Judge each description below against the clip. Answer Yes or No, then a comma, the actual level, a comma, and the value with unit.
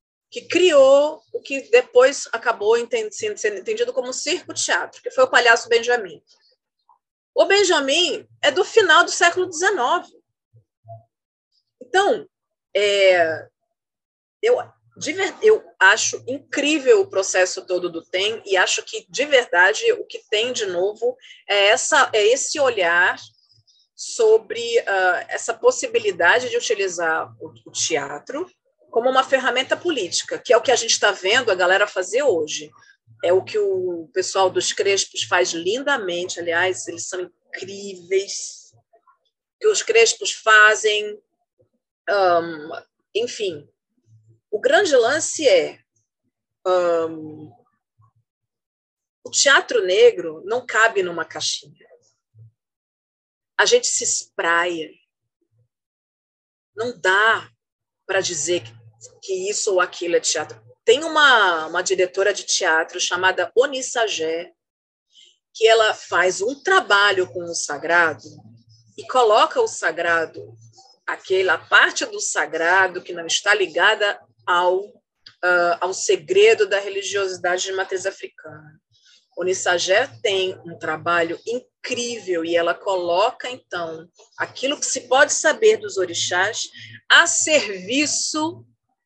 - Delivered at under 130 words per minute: Yes, slow, 120 wpm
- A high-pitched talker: Yes, high, 220 Hz